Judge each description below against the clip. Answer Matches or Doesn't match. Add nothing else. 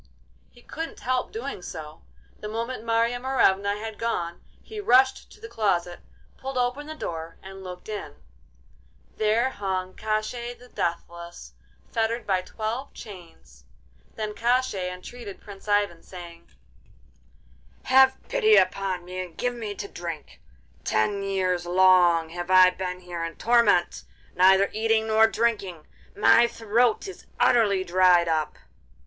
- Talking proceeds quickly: Doesn't match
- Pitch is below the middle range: Doesn't match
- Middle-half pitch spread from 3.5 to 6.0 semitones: Matches